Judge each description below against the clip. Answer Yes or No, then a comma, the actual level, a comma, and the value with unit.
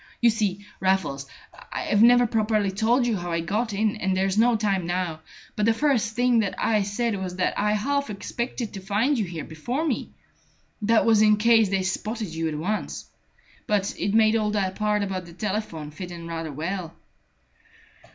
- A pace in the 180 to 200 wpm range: Yes, average, 190 wpm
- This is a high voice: Yes, high, 210 Hz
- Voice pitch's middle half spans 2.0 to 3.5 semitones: Yes, average, 3.2 semitones